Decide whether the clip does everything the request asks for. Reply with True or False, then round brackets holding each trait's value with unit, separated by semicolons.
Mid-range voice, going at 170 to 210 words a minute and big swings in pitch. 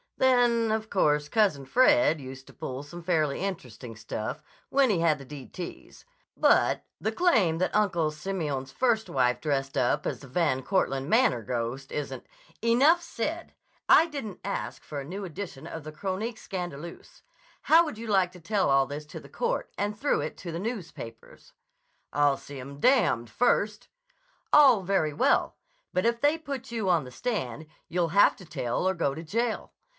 True (175 Hz; 180 wpm; 8.1 semitones)